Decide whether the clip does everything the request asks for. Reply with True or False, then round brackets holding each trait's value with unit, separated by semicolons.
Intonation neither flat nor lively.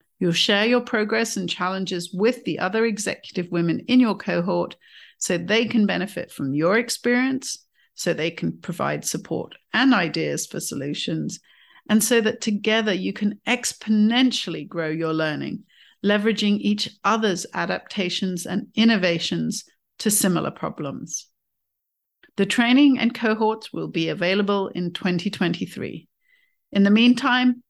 True (4.5 semitones)